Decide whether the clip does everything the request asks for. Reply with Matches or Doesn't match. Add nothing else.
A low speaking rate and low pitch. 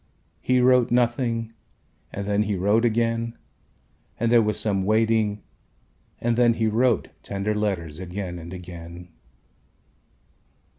Matches